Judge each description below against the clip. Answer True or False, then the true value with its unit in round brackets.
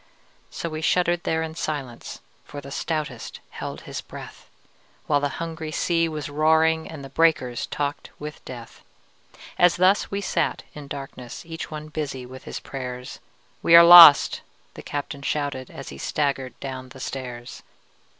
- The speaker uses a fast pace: False (160 wpm)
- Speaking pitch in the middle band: True (150 Hz)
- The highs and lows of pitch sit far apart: False (3.4 semitones)